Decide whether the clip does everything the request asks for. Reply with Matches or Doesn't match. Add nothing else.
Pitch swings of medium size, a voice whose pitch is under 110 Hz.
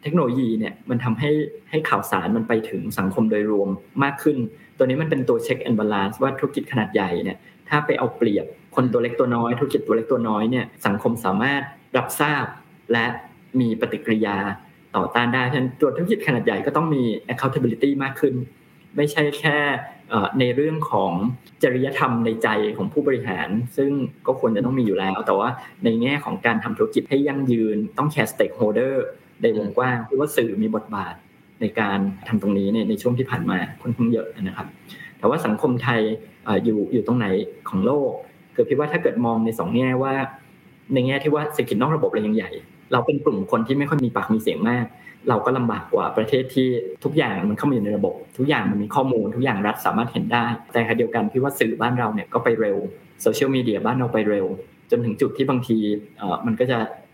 Doesn't match